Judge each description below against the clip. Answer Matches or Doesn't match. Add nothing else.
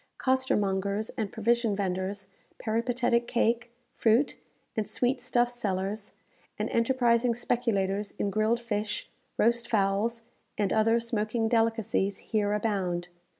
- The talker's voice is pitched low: Doesn't match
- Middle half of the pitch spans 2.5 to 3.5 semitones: Matches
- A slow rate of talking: Matches